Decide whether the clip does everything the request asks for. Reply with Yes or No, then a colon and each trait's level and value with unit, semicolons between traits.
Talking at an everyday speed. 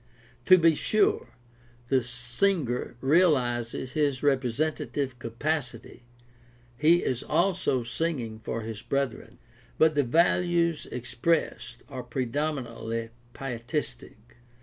No: slow, 105 wpm